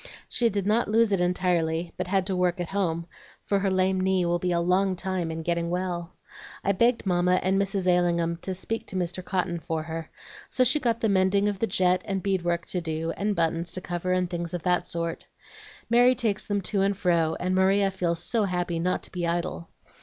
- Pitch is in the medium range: Yes, medium, 180 Hz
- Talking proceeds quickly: Yes, fast, 220 wpm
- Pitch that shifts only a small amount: Yes, narrow, 2.3 semitones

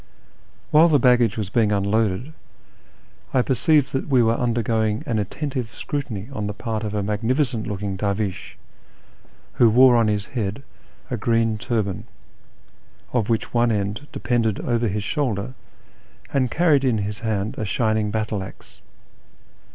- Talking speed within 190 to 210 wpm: No, average, 145 wpm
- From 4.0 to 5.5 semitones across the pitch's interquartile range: No, average, 3.1 semitones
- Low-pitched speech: Yes, low, 110 Hz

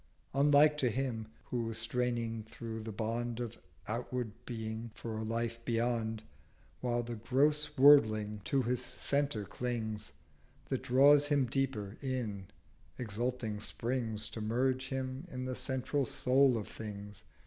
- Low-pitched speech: Yes, low, 120 Hz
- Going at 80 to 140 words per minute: Yes, slow, 135 wpm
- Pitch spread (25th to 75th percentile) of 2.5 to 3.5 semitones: Yes, average, 2.9 semitones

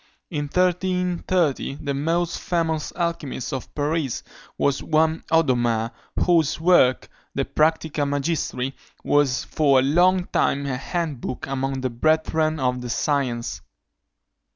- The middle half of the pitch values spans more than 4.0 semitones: No, average, 3.7 semitones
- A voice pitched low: No, medium, 150 Hz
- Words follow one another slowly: Yes, slow, 125 wpm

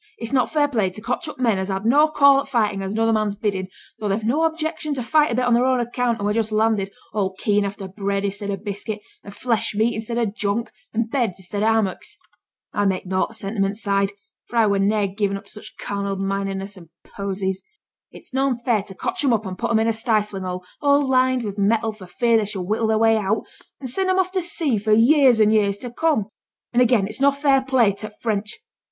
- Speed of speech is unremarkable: No, fast, 245 wpm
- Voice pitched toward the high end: Yes, high, 220 Hz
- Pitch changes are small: No, average, 3.6 semitones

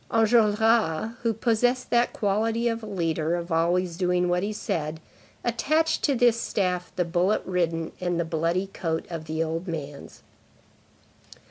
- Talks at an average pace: Yes, average, 145 wpm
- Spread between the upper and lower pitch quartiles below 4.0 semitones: No, average, 5.3 semitones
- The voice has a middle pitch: Yes, medium, 180 Hz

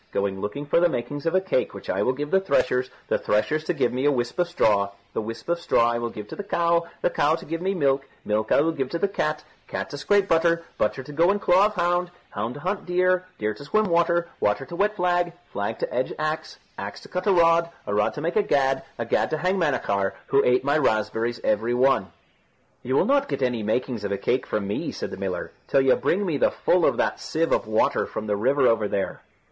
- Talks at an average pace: No, fast, 255 wpm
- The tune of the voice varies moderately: No, wide, 6.8 semitones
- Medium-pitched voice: Yes, medium, 145 Hz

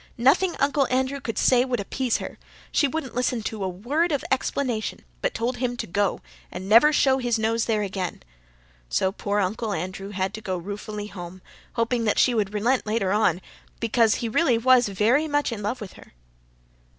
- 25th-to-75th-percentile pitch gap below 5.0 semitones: Yes, average, 4.1 semitones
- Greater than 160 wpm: Yes, average, 190 wpm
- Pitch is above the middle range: Yes, high, 230 Hz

